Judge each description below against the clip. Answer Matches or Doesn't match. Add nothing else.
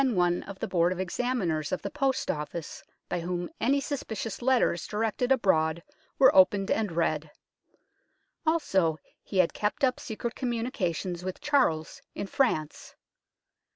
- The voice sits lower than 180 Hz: Doesn't match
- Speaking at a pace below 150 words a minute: Matches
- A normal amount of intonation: Doesn't match